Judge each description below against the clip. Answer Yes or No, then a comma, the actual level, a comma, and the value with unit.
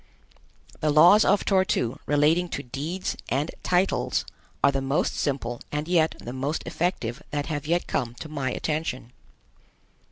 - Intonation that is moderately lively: Yes, average, 4.1 semitones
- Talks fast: No, average, 155 wpm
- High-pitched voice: No, medium, 150 Hz